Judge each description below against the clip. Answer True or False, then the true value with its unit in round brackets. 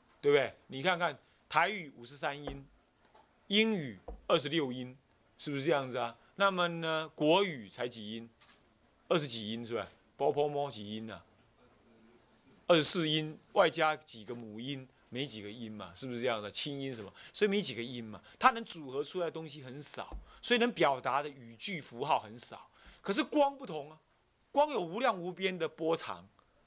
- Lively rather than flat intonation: True (6.0 semitones)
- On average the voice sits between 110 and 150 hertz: True (140 Hz)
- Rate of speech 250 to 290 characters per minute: True (260 characters per minute)